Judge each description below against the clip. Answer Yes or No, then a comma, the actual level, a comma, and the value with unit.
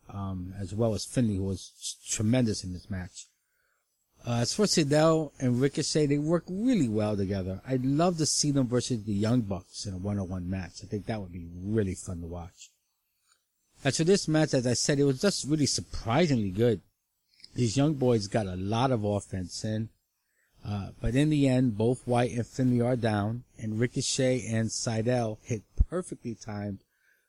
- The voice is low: Yes, low, 115 Hz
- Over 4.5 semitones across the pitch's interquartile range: Yes, average, 5.1 semitones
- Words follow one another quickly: No, average, 190 wpm